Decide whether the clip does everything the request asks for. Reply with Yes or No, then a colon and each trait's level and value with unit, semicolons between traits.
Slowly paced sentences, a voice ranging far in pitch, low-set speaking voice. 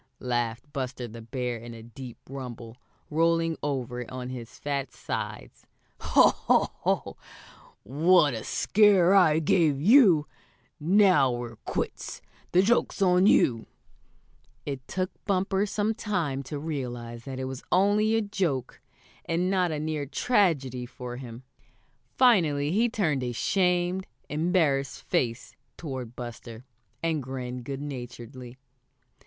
No: slow, 130 wpm; wide, 6.3 semitones; medium, 145 Hz